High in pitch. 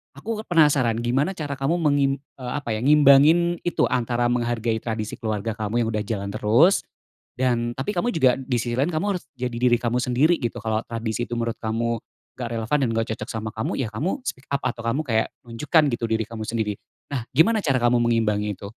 No: low, 120 Hz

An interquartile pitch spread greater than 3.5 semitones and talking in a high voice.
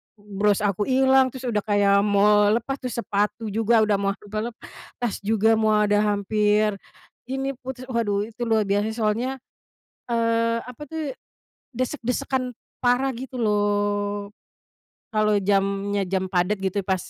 No: average, 3.0 semitones; high, 215 Hz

